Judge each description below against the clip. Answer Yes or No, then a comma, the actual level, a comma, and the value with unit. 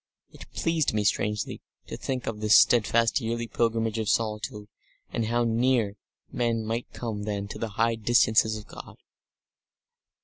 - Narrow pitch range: Yes, narrow, 1.7 semitones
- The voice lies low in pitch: Yes, low, 115 Hz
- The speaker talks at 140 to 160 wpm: Yes, average, 150 wpm